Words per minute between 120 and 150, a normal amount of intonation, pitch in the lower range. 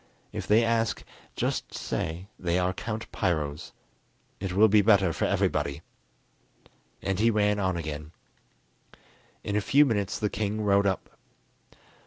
Yes: average, 140 wpm; average, 3.1 semitones; low, 100 Hz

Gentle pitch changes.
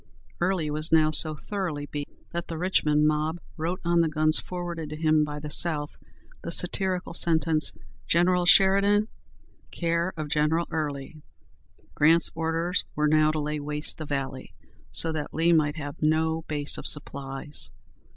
Yes: narrow, 2.1 semitones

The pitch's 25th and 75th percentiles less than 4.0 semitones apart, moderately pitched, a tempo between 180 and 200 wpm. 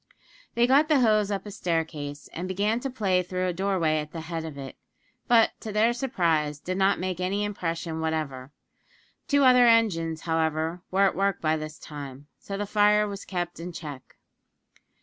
No: average, 4.6 semitones; medium, 180 Hz; average, 185 wpm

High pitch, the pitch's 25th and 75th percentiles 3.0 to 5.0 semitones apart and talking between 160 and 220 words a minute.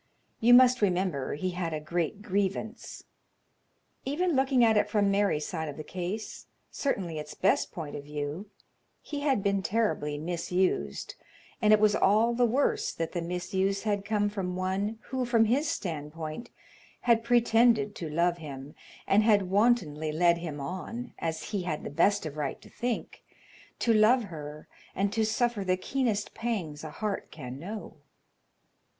No: high, 195 Hz; wide, 5.4 semitones; average, 165 wpm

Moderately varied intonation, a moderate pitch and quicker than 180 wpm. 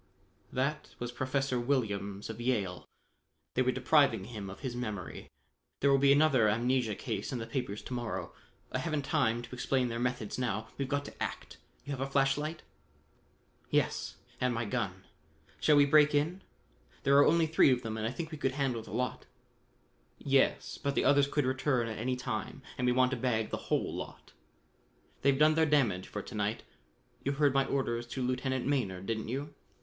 No: average, 3.3 semitones; low, 130 Hz; average, 195 wpm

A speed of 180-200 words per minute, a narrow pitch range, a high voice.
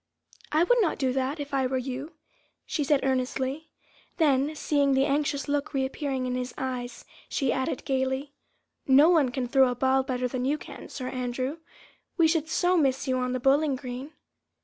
Yes: average, 195 wpm; narrow, 2.2 semitones; very high, 270 Hz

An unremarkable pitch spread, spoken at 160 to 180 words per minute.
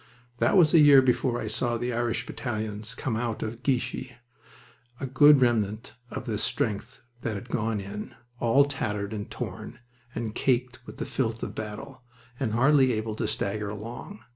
Yes: average, 3.2 semitones; average, 170 wpm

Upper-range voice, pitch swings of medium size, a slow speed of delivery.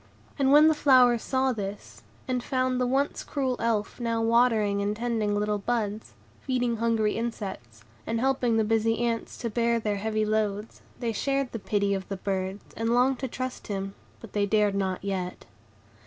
No: high, 225 Hz; average, 3.2 semitones; average, 180 wpm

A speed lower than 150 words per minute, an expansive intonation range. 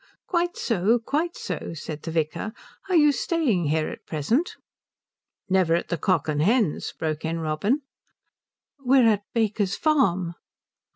Yes: average, 140 wpm; wide, 8.3 semitones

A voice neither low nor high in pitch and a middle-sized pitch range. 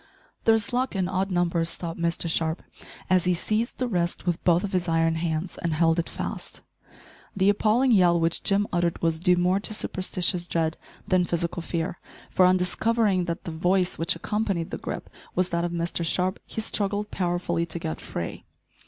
No: medium, 175 Hz; narrow, 2.3 semitones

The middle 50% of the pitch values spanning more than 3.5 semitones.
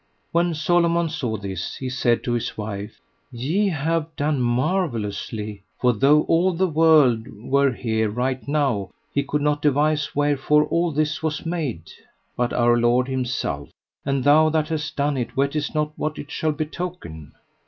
Yes: average, 4.5 semitones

